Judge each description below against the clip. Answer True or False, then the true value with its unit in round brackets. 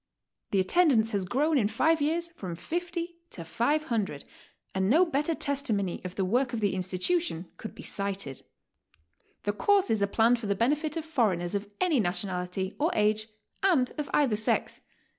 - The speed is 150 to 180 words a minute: True (165 wpm)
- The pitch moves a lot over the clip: True (7.9 semitones)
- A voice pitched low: False (225 Hz)